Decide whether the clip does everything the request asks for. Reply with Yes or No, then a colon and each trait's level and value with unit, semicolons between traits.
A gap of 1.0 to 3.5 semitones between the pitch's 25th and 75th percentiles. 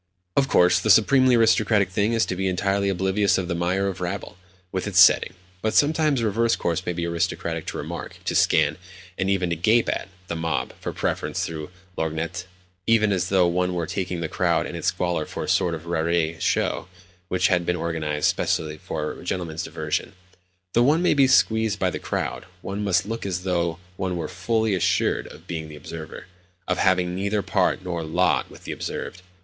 Yes: average, 3.0 semitones